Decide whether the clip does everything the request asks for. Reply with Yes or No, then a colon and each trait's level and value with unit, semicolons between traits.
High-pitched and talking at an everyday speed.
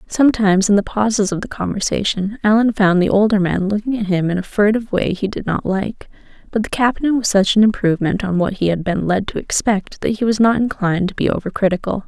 No: high, 205 Hz; fast, 235 wpm